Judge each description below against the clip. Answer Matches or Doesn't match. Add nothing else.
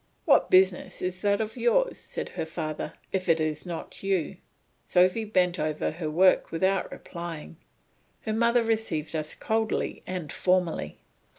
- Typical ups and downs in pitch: Matches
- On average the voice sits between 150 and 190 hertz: Matches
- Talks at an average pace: Matches